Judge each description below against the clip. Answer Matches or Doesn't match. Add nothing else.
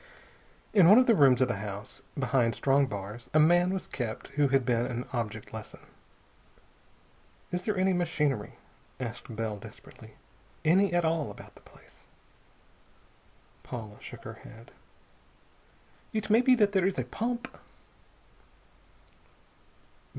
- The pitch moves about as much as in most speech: Doesn't match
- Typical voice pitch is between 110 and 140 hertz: Matches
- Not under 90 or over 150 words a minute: Matches